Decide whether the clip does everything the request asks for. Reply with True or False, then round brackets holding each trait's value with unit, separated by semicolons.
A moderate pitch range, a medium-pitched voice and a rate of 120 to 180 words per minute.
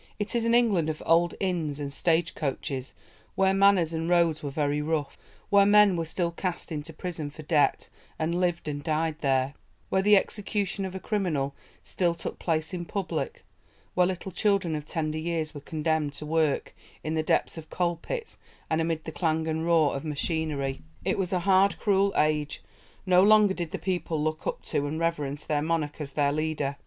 False (3.3 semitones; 165 Hz; 190 wpm)